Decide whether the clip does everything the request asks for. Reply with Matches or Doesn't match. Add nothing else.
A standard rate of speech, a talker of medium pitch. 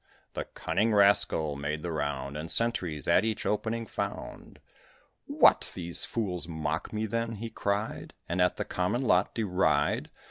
Doesn't match